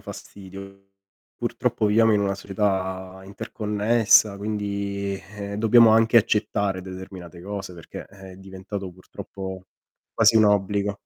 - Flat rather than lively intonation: Yes, narrow, 1.7 semitones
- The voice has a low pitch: Yes, low, 100 Hz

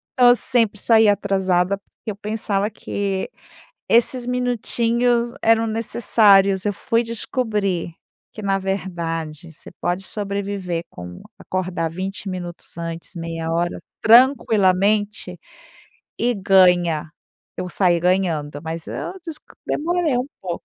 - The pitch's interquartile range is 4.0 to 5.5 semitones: Yes, average, 4.3 semitones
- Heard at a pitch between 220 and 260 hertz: No, high, 195 Hz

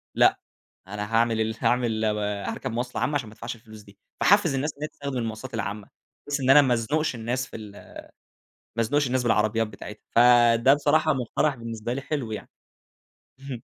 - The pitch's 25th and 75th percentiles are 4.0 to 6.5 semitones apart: No, average, 3.6 semitones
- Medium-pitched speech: No, low, 120 Hz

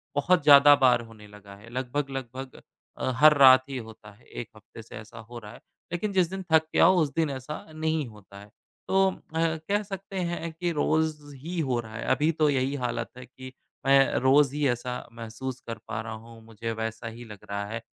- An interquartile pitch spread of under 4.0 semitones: No, wide, 5.5 semitones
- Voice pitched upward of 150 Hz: No, low, 130 Hz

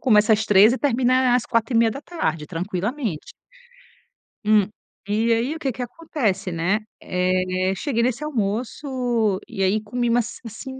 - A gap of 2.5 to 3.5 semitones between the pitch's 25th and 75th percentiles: No, average, 4.3 semitones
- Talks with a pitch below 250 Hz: Yes, high, 225 Hz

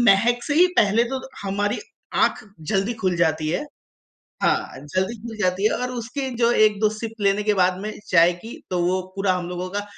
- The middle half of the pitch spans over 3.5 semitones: Yes, average, 3.9 semitones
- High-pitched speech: Yes, high, 200 Hz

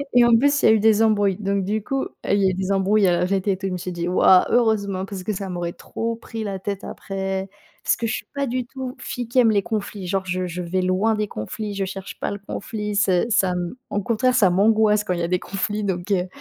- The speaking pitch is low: No, high, 200 Hz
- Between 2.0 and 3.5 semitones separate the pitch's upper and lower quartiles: Yes, average, 2.8 semitones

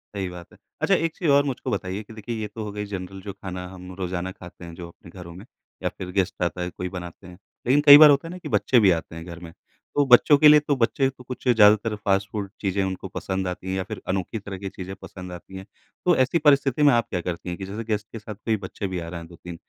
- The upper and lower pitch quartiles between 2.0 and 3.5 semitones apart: No, average, 4.3 semitones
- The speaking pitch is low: Yes, very low, 95 Hz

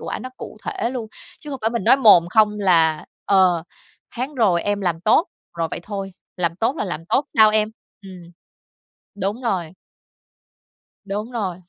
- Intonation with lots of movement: No, average, 4.3 semitones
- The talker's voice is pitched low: No, high, 200 Hz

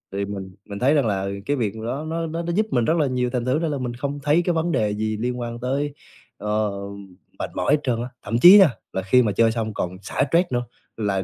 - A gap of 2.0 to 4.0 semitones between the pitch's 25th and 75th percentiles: No, average, 5.3 semitones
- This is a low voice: Yes, low, 125 Hz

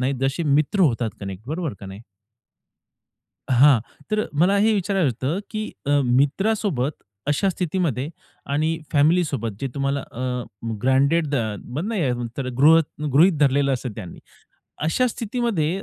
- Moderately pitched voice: Yes, medium, 145 Hz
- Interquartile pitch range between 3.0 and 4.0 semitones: No, wide, 5.6 semitones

